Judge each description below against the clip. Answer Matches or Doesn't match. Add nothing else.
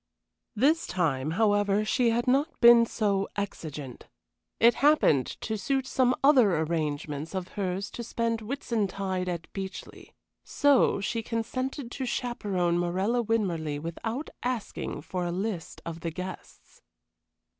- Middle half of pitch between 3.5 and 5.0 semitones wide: Doesn't match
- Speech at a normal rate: Doesn't match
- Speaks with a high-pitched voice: Matches